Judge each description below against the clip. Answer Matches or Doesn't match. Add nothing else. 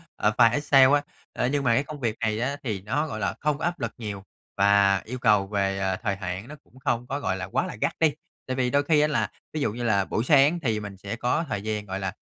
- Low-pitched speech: Matches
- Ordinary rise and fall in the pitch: Doesn't match